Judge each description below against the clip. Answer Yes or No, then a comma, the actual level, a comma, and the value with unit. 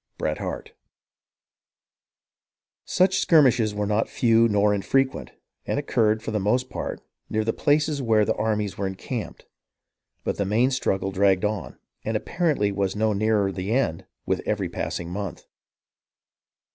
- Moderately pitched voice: No, low, 110 Hz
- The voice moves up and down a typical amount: Yes, average, 3.9 semitones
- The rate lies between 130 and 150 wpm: Yes, average, 145 wpm